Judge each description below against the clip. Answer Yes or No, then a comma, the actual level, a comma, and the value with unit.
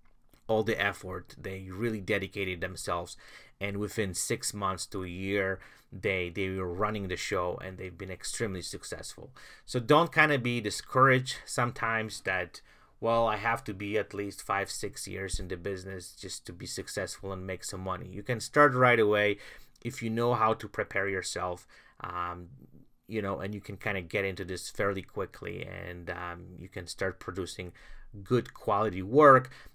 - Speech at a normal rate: Yes, average, 180 wpm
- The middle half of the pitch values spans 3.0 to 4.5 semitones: Yes, average, 3.5 semitones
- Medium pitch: No, low, 100 Hz